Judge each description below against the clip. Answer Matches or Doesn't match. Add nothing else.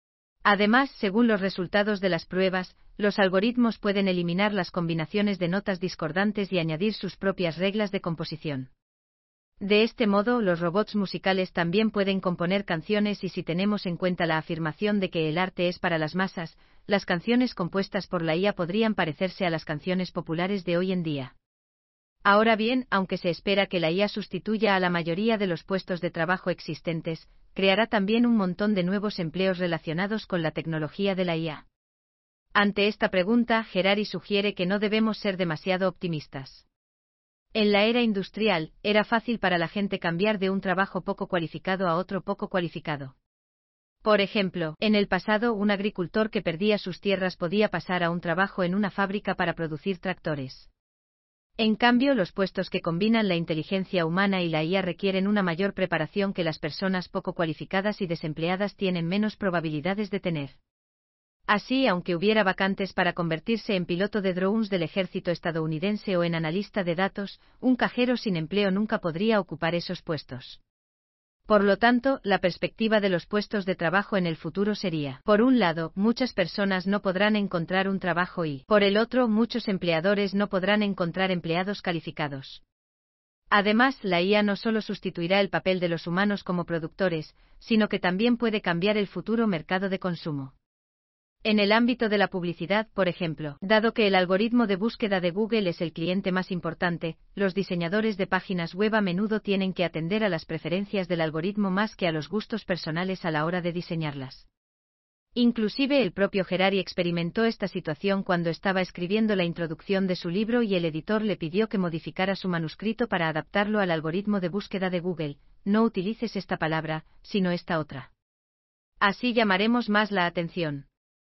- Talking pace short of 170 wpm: Doesn't match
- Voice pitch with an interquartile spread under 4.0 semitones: Matches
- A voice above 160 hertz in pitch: Matches